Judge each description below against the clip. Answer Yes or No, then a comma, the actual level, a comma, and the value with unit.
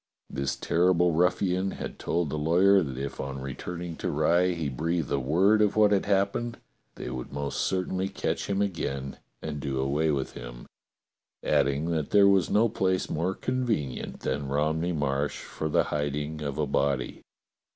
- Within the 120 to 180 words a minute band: Yes, average, 170 wpm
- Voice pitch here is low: Yes, very low, 80 Hz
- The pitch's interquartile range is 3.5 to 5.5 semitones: Yes, average, 5.0 semitones